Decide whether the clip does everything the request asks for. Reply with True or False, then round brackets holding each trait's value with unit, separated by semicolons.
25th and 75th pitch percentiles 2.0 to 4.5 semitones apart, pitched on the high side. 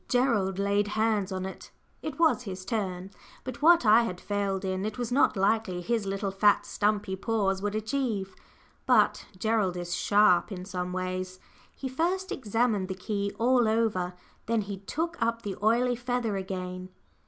True (3.4 semitones; 205 Hz)